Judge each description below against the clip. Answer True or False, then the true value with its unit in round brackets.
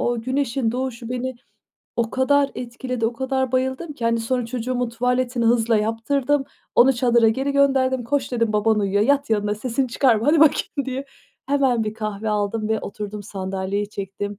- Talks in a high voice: True (240 Hz)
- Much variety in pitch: False (3.0 semitones)